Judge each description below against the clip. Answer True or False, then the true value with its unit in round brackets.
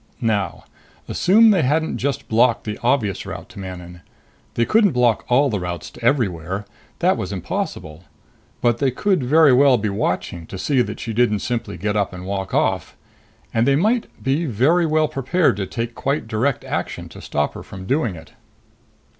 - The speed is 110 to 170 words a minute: False (180 wpm)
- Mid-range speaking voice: False (115 Hz)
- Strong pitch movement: True (6.5 semitones)